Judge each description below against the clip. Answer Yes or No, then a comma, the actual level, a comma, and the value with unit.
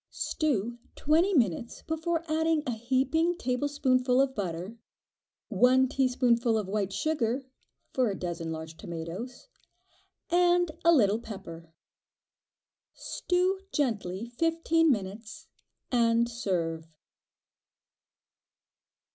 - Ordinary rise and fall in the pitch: No, wide, 7.5 semitones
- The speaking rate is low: Yes, slow, 95 wpm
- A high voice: Yes, high, 245 Hz